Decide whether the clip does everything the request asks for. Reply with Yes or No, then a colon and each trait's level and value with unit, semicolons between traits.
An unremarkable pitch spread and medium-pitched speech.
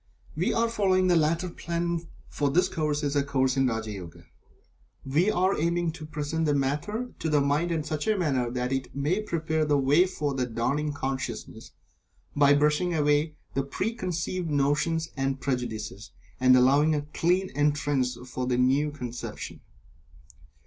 Yes: average, 3.9 semitones; medium, 150 Hz